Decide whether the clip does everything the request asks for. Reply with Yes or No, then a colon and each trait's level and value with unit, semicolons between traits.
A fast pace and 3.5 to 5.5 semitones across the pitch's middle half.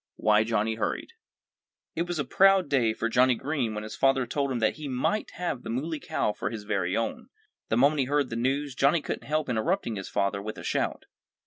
Yes: fast, 225 wpm; average, 4.9 semitones